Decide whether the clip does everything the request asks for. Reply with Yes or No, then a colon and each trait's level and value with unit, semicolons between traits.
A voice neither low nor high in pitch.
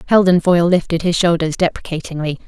Yes: medium, 170 Hz